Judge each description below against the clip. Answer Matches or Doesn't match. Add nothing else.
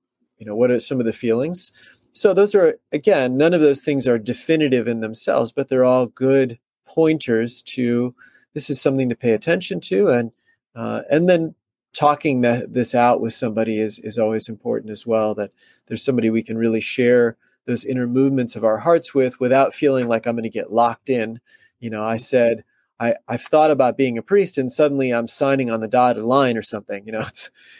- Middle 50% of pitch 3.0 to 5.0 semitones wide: Matches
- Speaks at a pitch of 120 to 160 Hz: Matches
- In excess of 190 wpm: Matches